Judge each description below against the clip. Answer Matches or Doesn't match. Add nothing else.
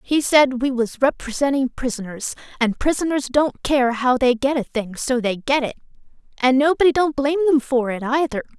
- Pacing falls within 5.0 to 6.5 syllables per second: Matches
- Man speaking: Doesn't match